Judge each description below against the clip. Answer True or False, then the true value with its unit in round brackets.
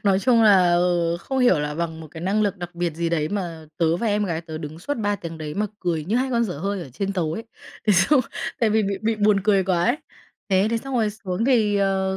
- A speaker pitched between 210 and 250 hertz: False (190 Hz)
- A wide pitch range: False (3.9 semitones)